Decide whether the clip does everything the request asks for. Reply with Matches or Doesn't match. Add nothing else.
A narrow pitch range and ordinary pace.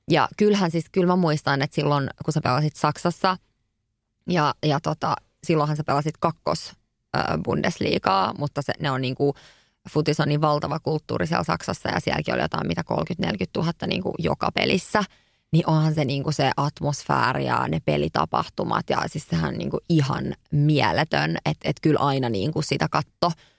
Doesn't match